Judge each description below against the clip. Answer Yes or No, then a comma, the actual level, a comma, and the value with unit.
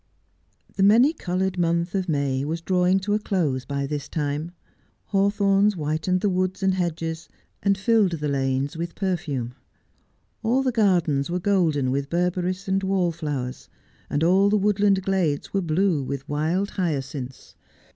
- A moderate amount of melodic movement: Yes, average, 4.7 semitones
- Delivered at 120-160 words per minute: Yes, average, 150 wpm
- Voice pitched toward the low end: No, medium, 175 Hz